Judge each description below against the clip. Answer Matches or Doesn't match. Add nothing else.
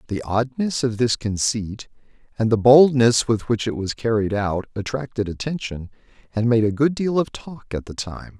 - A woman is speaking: Doesn't match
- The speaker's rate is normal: Matches